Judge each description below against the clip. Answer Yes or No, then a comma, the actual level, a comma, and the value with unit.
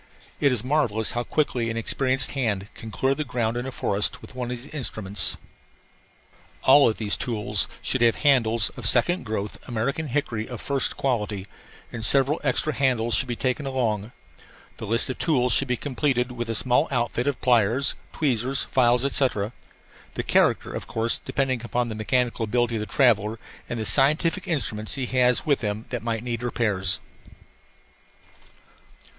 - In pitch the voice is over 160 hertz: No, low, 120 Hz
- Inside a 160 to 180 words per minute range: Yes, average, 170 wpm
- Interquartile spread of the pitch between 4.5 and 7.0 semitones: No, average, 3.2 semitones